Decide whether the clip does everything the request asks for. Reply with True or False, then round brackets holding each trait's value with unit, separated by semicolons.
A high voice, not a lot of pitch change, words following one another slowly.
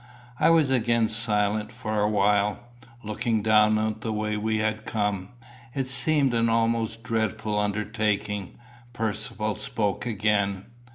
False (110 Hz; 1.4 semitones; 130 wpm)